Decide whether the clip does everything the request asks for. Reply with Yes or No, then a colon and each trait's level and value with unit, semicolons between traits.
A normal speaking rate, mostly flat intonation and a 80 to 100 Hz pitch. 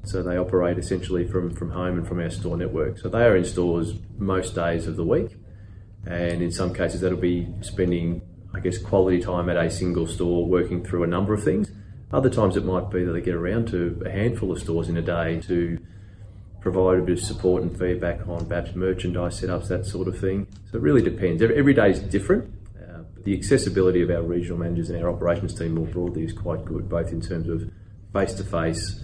No: fast, 225 wpm; narrow, 2.3 semitones; very low, 90 Hz